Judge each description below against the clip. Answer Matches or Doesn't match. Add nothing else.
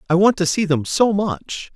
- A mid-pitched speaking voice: Matches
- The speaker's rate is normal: Doesn't match